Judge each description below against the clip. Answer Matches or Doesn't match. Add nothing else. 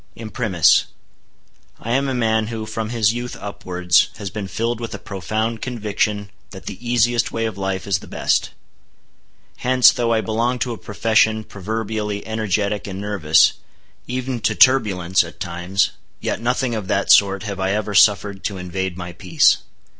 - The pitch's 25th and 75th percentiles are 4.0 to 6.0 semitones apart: Doesn't match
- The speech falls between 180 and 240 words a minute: Doesn't match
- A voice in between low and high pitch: Doesn't match